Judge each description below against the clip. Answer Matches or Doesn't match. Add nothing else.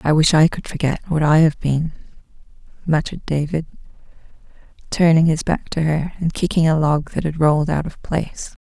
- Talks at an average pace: Matches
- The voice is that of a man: Doesn't match